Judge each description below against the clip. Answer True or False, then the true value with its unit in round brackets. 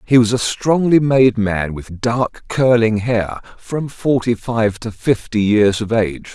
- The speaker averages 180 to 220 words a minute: False (170 wpm)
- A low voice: True (115 Hz)